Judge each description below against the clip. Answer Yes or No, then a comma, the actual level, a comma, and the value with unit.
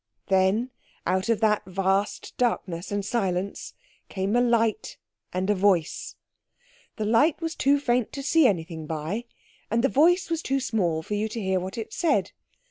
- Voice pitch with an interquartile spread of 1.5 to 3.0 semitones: No, average, 4.6 semitones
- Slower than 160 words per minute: No, average, 170 wpm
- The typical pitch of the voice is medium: No, high, 210 Hz